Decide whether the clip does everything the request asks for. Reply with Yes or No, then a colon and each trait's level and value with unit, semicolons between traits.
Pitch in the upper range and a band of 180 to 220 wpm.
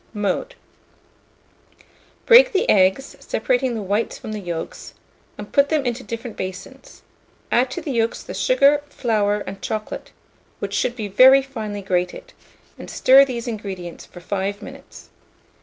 No: high, 225 Hz; average, 145 wpm